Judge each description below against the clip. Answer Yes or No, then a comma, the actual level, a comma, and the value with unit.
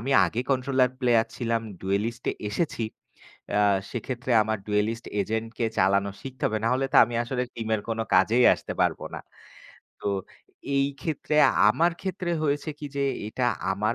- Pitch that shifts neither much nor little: Yes, average, 3.4 semitones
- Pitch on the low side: Yes, low, 120 Hz